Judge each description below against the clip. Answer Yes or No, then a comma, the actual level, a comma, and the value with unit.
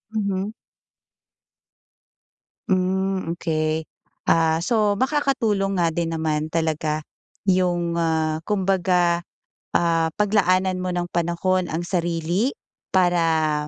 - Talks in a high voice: No, medium, 175 Hz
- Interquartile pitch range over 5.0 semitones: No, average, 2.7 semitones